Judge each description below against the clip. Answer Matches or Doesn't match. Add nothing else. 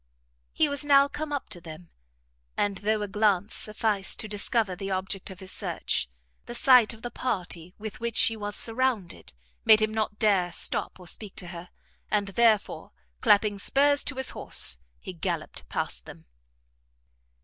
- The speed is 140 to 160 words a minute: Doesn't match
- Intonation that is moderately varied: Matches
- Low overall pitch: Doesn't match